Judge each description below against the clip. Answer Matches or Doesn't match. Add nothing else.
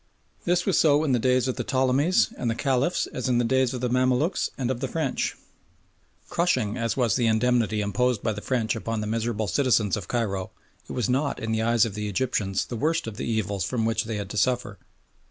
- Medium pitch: Doesn't match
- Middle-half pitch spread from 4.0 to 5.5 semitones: Doesn't match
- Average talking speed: Doesn't match